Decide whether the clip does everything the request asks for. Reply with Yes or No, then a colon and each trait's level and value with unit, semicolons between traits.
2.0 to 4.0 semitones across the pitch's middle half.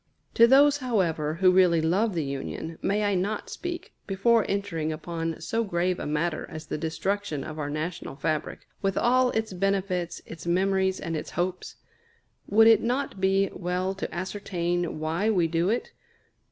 Yes: average, 3.7 semitones